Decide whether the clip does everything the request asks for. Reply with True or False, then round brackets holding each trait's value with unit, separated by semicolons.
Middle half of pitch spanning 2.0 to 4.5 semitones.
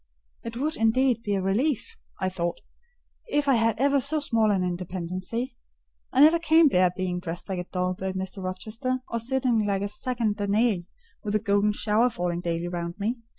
False (5.2 semitones)